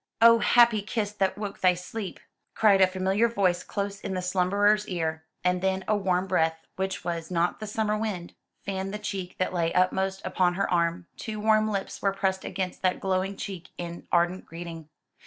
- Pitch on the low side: No, high, 190 Hz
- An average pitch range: No, narrow, 2.3 semitones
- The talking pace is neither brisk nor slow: Yes, average, 190 wpm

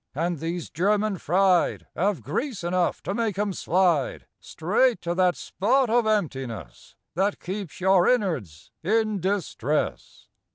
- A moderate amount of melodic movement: Yes, average, 3.9 semitones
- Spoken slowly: Yes, slow, 130 wpm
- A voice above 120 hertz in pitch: Yes, medium, 185 Hz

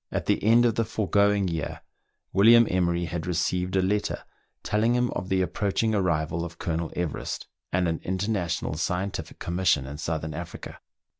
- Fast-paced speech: No, average, 165 wpm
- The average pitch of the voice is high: No, very low, 90 Hz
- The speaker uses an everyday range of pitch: Yes, average, 3.5 semitones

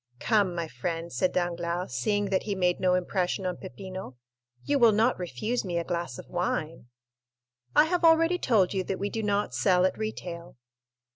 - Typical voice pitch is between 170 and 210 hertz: Yes, medium, 185 Hz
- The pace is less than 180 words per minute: No, average, 185 wpm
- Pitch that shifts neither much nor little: Yes, average, 3.4 semitones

